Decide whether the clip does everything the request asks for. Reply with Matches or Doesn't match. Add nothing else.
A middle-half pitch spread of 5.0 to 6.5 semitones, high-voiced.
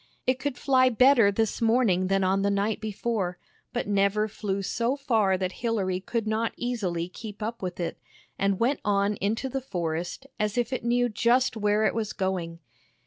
Doesn't match